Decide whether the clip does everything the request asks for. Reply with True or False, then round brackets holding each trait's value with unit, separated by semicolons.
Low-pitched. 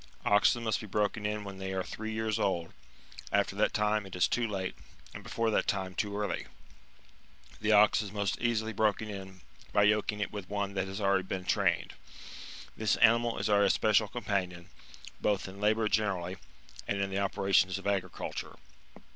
True (100 Hz)